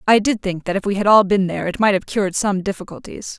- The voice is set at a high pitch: Yes, high, 200 Hz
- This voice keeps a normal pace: No, fast, 285 wpm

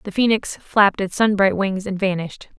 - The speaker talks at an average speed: Yes, average, 185 wpm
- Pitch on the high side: Yes, high, 200 Hz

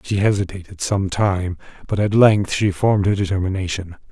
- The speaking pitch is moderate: No, very low, 95 Hz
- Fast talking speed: No, average, 160 wpm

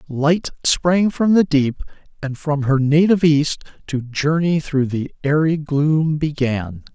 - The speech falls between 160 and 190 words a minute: No, average, 145 wpm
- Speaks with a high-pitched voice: No, medium, 150 Hz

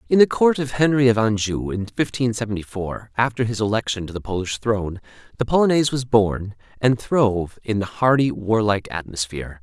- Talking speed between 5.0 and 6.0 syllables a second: Yes, 5.6 syllables/s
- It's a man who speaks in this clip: Yes, male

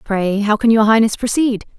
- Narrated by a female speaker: Yes, female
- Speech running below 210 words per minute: Yes, average, 200 wpm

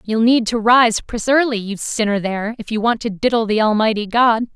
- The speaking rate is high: Yes, fast, 225 wpm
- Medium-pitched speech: No, high, 225 Hz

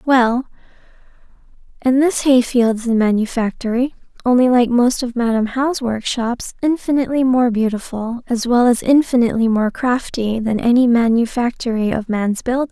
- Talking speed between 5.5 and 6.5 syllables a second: No, 5.0 syllables/s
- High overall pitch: Yes, high, 240 Hz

